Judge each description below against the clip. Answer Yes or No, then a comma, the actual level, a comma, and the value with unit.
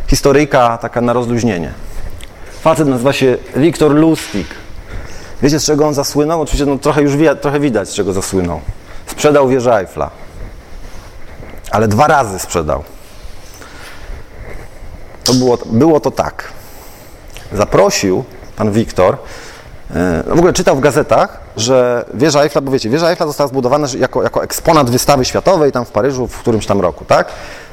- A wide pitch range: Yes, wide, 6.2 semitones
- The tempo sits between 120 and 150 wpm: Yes, average, 145 wpm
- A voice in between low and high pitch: No, low, 125 Hz